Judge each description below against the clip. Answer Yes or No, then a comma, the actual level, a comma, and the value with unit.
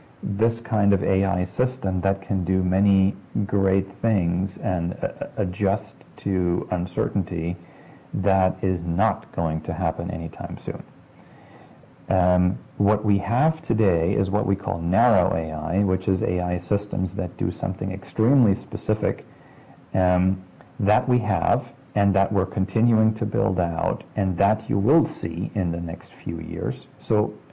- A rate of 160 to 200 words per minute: No, average, 145 wpm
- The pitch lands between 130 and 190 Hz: No, very low, 95 Hz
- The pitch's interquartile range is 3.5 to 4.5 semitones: No, average, 2.8 semitones